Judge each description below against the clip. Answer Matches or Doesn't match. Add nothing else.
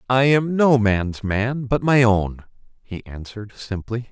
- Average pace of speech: Matches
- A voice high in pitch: Doesn't match